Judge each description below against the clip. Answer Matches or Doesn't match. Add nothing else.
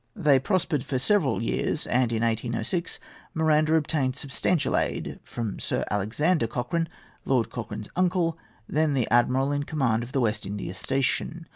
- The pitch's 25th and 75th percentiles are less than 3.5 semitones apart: Doesn't match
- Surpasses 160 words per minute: Doesn't match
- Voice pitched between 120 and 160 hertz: Matches